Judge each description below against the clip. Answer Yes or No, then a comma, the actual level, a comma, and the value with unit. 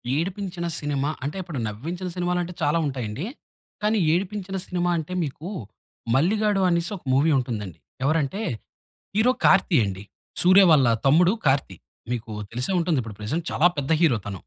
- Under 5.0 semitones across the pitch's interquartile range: No, wide, 5.4 semitones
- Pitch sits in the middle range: Yes, medium, 160 Hz